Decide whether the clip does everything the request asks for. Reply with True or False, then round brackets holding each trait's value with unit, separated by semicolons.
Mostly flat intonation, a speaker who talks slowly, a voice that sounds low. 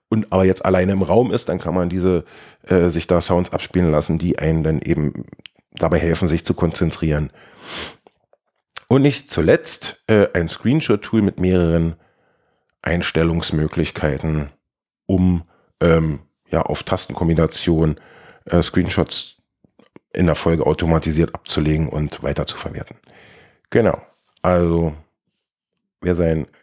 True (2.3 semitones; 120 wpm; 85 Hz)